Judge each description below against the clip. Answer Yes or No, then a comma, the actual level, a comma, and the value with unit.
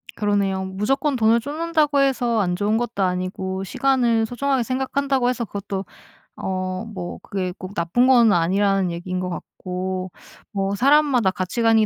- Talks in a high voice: Yes, high, 210 Hz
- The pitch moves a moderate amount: Yes, average, 5.0 semitones